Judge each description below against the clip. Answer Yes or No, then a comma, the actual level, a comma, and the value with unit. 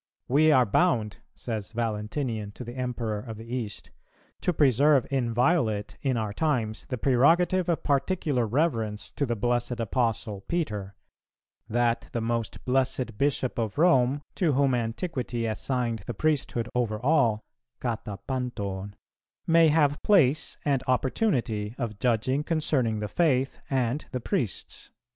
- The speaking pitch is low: Yes, low, 125 Hz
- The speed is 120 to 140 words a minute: Yes, slow, 135 wpm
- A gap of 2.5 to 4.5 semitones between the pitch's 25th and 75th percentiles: Yes, average, 4.1 semitones